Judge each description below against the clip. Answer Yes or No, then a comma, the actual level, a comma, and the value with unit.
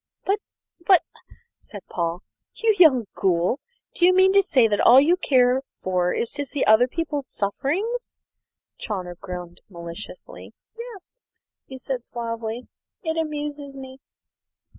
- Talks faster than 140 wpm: No, slow, 135 wpm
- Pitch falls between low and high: No, very high, 260 Hz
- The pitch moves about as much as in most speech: No, wide, 7.9 semitones